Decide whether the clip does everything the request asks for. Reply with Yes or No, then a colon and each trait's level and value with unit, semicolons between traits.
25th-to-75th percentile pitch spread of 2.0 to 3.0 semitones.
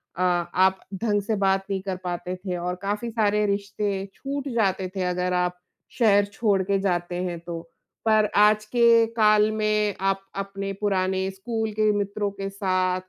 Yes: narrow, 2.4 semitones